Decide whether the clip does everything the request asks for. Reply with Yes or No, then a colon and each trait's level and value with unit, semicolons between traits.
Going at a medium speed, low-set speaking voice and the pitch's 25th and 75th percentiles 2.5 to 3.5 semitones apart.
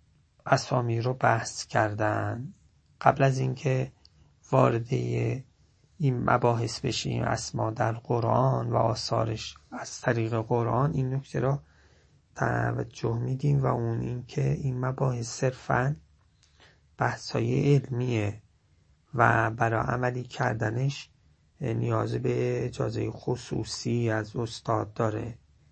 No: slow, 100 wpm; low, 115 Hz; average, 3.2 semitones